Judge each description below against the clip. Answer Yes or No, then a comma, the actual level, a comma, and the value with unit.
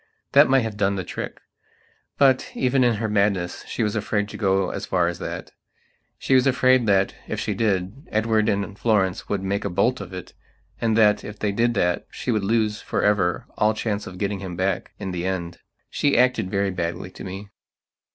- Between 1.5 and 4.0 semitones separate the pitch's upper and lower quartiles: Yes, average, 3.0 semitones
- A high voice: No, low, 105 Hz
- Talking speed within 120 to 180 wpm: No, fast, 205 wpm